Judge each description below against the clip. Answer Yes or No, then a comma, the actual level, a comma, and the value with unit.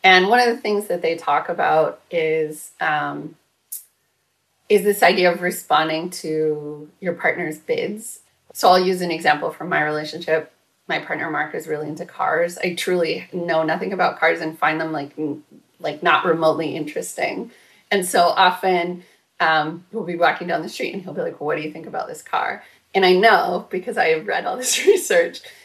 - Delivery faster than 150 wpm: Yes, average, 190 wpm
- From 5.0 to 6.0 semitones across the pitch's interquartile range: Yes, wide, 5.6 semitones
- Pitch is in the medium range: Yes, medium, 180 Hz